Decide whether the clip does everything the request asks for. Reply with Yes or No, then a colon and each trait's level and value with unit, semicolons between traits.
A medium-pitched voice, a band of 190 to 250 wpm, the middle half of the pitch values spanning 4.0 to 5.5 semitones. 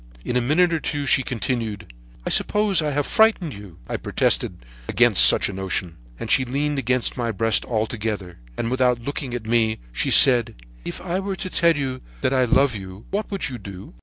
No: low, 125 Hz; average, 200 wpm; average, 4.9 semitones